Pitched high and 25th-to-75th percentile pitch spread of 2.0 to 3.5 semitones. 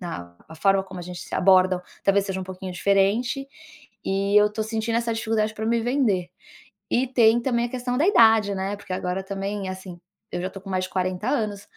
Yes: high, 200 Hz; average, 3.2 semitones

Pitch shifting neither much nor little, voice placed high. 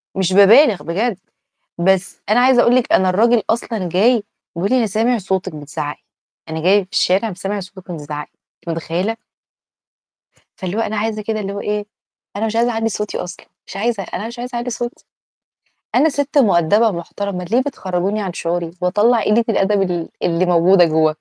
Yes: average, 4.1 semitones; high, 200 Hz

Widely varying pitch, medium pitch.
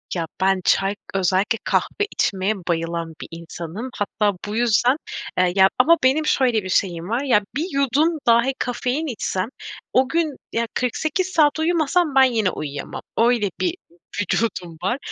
No: wide, 6.4 semitones; high, 230 Hz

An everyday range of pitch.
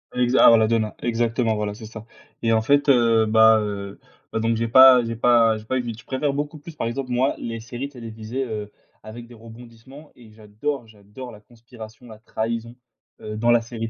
No: narrow, 1.9 semitones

